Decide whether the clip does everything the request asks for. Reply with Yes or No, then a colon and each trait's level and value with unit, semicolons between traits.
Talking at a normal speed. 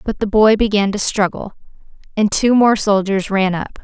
Yes: average, 190 wpm